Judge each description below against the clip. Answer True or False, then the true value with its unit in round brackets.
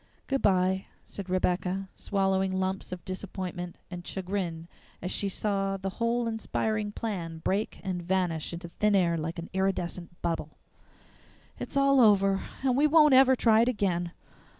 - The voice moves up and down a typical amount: True (3.0 semitones)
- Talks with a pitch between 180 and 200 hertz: True (190 Hz)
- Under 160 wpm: True (150 wpm)